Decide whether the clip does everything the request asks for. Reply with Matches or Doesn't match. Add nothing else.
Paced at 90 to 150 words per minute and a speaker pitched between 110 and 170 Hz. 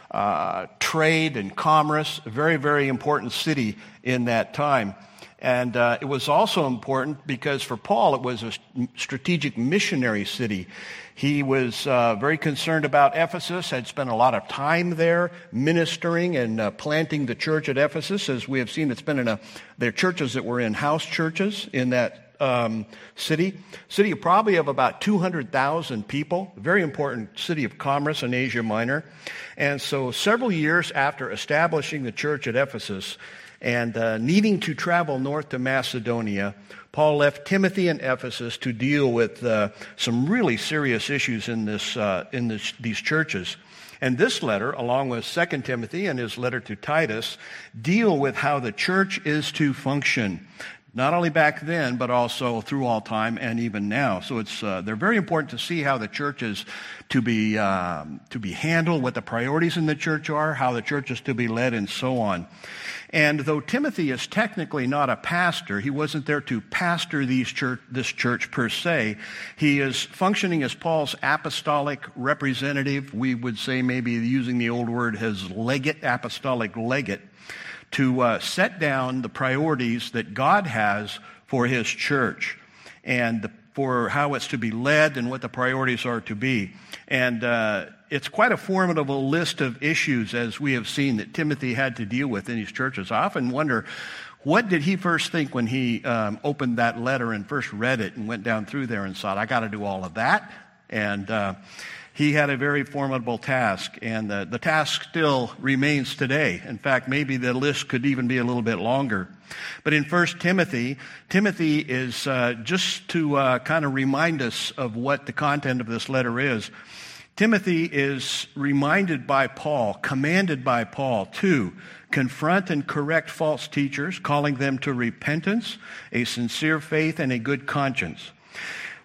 Doesn't match